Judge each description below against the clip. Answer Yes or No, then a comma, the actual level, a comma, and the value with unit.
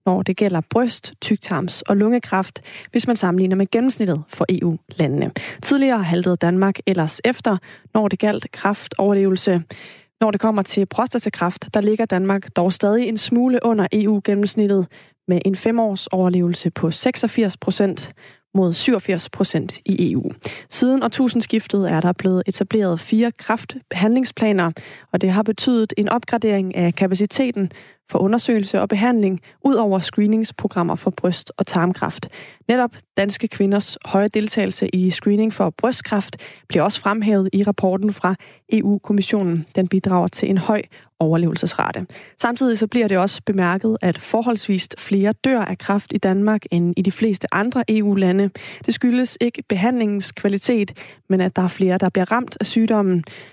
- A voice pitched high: Yes, high, 200 Hz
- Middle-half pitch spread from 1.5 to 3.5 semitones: Yes, average, 3.2 semitones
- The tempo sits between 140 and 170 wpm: Yes, average, 150 wpm